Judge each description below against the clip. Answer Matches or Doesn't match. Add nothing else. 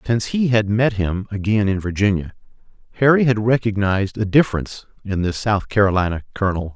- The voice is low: Matches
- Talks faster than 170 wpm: Doesn't match